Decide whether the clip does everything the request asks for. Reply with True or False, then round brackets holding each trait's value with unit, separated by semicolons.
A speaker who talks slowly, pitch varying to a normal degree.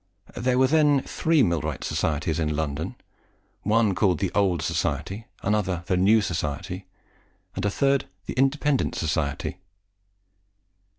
False (125 wpm; 7.4 semitones)